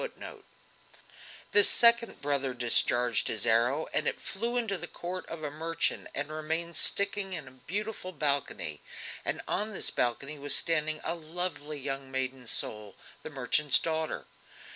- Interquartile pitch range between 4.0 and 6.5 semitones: Yes, average, 5.0 semitones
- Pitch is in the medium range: Yes, medium, 155 Hz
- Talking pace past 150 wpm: No, average, 145 wpm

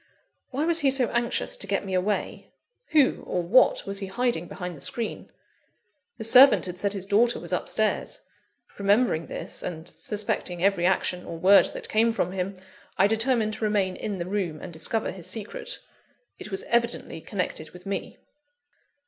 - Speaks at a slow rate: No, average, 175 wpm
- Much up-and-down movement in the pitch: No, average, 3.9 semitones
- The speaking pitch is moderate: No, high, 200 Hz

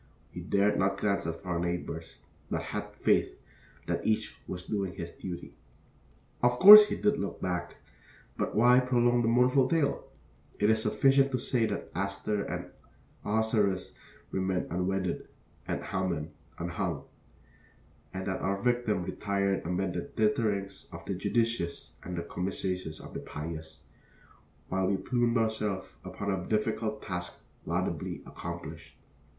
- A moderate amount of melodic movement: Yes, average, 3.9 semitones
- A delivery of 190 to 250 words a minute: No, average, 140 wpm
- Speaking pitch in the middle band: No, low, 100 Hz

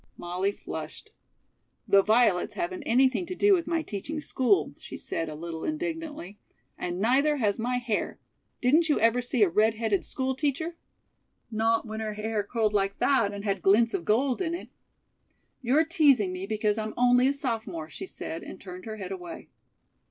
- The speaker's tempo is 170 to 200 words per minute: Yes, average, 180 wpm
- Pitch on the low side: No, high, 225 Hz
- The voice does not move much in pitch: No, wide, 5.6 semitones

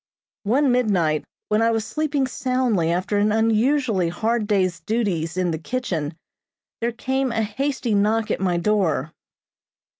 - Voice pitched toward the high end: Yes, high, 215 Hz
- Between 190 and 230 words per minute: No, average, 145 wpm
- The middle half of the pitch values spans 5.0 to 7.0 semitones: Yes, average, 5.3 semitones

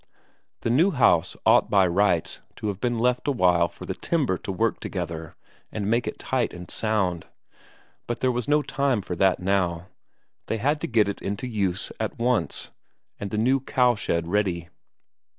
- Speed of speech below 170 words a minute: No, average, 180 wpm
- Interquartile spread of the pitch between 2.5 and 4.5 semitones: No, average, 5.1 semitones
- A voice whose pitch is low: Yes, low, 105 Hz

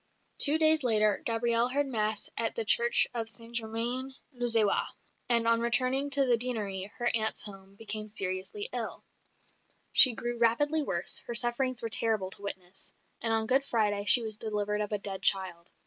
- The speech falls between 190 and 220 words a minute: No, average, 175 wpm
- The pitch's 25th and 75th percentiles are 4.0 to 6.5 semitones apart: No, average, 3.2 semitones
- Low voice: No, high, 230 Hz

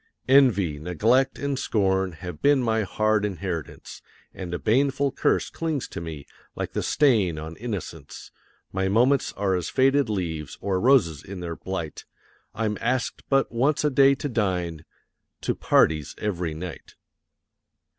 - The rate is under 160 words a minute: Yes, average, 145 wpm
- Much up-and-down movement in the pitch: Yes, wide, 7.0 semitones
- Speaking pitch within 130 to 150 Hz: No, low, 100 Hz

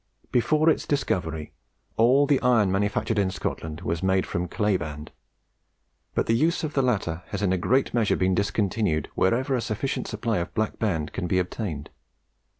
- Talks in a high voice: No, low, 100 Hz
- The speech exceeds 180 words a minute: No, average, 175 wpm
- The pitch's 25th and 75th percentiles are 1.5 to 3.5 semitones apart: No, average, 5.1 semitones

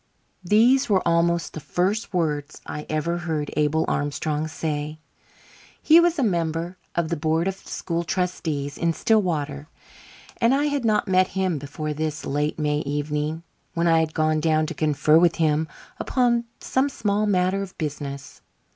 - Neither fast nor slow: Yes, average, 160 wpm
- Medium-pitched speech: Yes, medium, 165 Hz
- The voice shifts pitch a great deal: No, average, 3.8 semitones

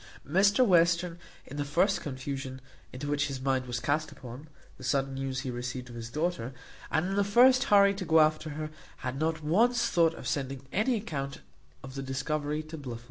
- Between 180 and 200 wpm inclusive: Yes, average, 195 wpm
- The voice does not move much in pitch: No, average, 4.5 semitones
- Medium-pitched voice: Yes, medium, 150 Hz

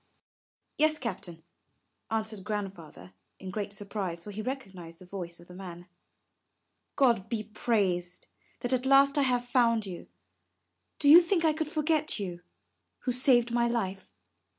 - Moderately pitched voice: No, high, 215 Hz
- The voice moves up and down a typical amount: No, wide, 5.7 semitones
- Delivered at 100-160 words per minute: Yes, average, 150 wpm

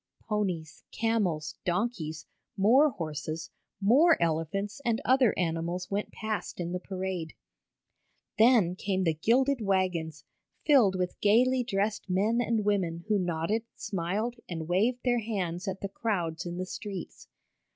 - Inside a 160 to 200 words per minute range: No, slow, 135 wpm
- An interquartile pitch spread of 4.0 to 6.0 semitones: Yes, average, 4.6 semitones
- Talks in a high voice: Yes, high, 195 Hz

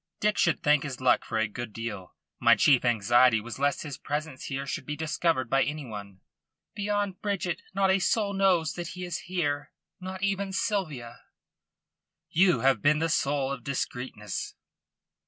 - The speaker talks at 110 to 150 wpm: No, average, 170 wpm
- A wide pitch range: Yes, wide, 6.6 semitones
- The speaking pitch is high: No, medium, 150 Hz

